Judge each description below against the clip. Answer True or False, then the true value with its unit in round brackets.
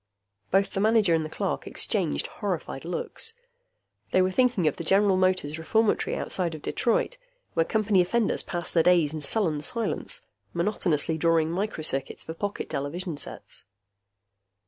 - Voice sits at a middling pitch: True (180 Hz)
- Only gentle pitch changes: False (4.2 semitones)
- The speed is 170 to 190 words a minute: False (145 wpm)